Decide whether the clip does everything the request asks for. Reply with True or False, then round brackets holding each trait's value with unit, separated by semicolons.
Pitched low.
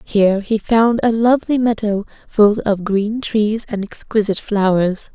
False (215 Hz)